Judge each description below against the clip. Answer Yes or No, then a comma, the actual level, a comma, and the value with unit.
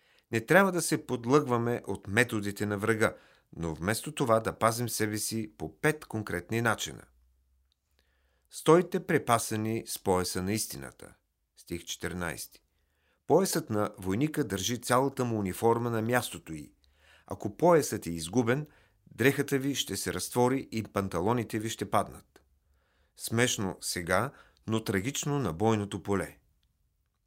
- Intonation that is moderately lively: No, wide, 6.2 semitones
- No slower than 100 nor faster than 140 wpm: Yes, average, 130 wpm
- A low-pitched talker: Yes, low, 105 Hz